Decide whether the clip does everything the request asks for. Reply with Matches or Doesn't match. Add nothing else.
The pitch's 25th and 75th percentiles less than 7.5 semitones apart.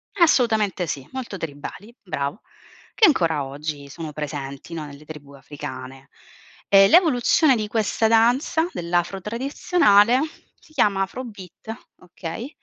Doesn't match